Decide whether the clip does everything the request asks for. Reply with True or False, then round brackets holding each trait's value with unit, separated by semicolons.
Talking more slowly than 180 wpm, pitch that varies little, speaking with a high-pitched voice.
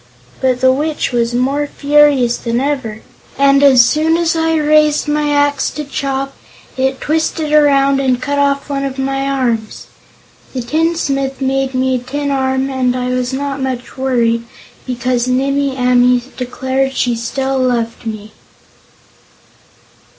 True (145 wpm; 2.1 semitones; 270 Hz)